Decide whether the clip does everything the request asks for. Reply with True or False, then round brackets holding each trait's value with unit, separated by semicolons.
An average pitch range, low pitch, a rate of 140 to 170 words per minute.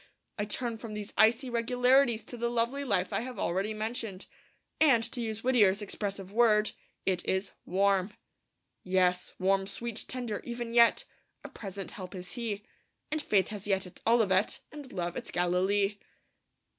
False (3.6 semitones; 210 Hz; 155 wpm)